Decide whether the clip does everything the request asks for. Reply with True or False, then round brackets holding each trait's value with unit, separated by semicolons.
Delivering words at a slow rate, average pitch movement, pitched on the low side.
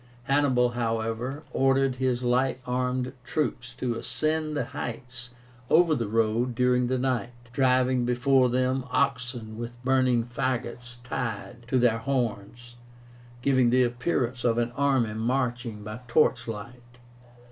False (125 wpm; 1.6 semitones; 125 Hz)